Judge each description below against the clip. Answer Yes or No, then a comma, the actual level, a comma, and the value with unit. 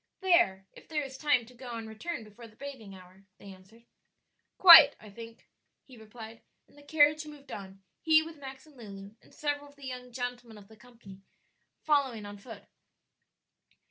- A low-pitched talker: No, high, 245 Hz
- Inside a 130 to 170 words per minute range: No, average, 180 wpm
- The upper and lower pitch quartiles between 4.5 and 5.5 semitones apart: Yes, average, 5.2 semitones